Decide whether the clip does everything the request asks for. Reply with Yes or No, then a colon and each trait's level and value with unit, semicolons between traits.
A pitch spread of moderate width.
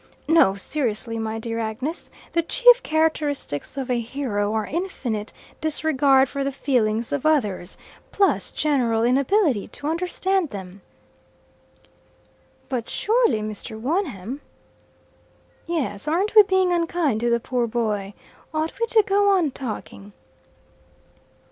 No: wide, 7.0 semitones